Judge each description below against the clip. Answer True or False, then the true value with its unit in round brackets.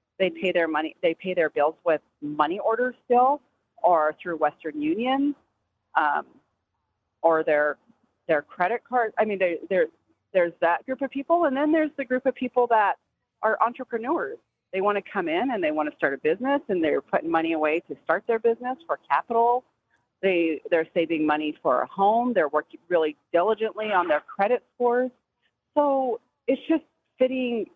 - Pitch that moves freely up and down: True (7.9 semitones)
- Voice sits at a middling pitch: False (220 Hz)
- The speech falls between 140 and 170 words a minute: False (180 wpm)